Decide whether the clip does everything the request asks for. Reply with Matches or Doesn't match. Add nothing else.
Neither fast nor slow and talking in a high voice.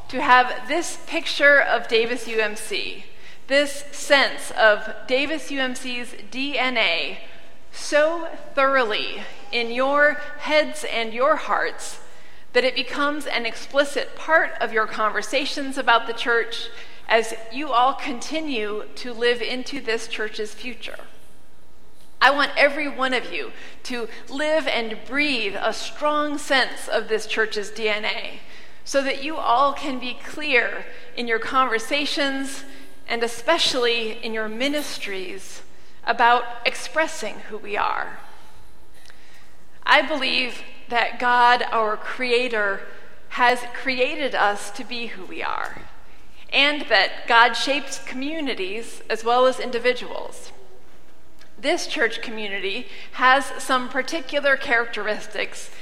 Doesn't match